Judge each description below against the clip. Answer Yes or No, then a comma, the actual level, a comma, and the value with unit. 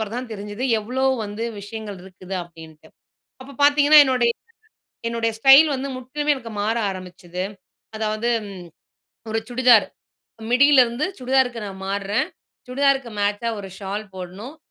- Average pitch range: Yes, average, 4.4 semitones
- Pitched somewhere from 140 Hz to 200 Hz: No, high, 230 Hz